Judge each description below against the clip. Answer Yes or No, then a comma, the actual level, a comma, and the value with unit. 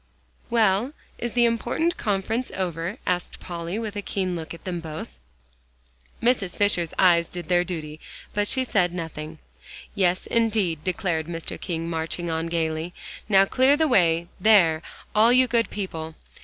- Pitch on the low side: No, medium, 180 Hz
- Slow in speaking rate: No, average, 155 wpm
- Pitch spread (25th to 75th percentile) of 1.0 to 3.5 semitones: No, average, 4.7 semitones